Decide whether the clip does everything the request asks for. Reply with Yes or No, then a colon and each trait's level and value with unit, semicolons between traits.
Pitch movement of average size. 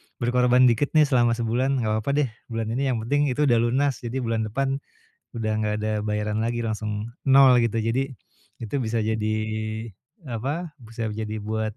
Yes: average, 3.2 semitones